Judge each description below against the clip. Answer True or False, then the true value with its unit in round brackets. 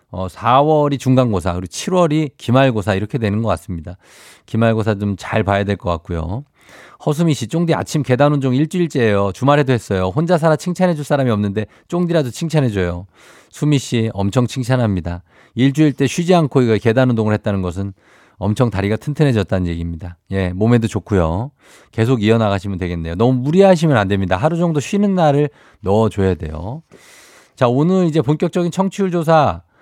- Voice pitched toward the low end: True (120 Hz)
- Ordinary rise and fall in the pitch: False (7.3 semitones)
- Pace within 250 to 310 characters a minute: False (380 characters per minute)